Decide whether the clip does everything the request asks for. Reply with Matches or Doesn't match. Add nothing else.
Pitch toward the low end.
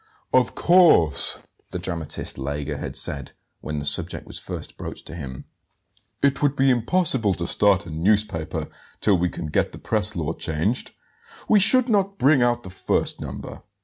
Matches